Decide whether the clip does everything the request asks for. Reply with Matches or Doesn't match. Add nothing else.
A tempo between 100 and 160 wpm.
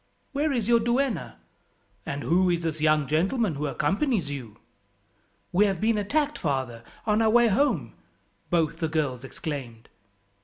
Matches